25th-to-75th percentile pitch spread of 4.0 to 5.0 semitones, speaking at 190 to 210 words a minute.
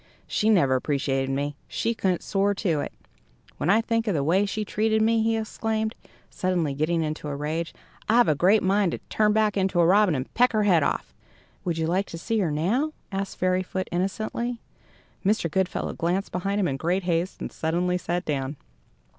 Yes: average, 4.7 semitones; average, 195 wpm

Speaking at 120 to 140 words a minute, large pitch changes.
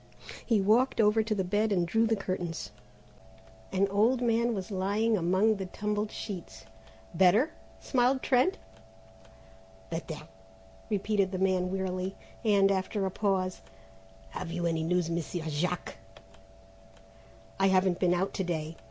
No: slow, 135 wpm; average, 3.2 semitones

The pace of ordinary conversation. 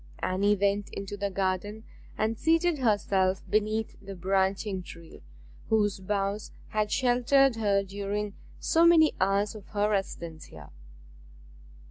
No: slow, 125 wpm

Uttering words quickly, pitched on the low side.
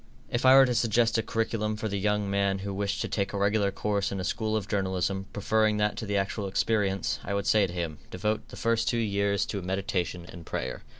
Yes: fast, 235 wpm; low, 100 Hz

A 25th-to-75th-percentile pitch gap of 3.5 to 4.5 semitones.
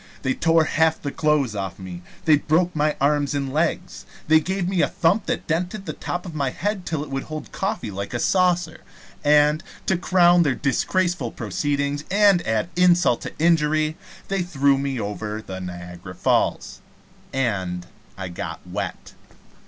No: average, 5.2 semitones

